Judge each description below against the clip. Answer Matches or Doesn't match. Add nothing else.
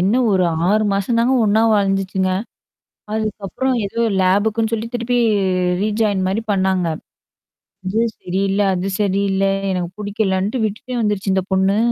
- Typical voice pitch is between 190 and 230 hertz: Matches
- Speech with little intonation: Matches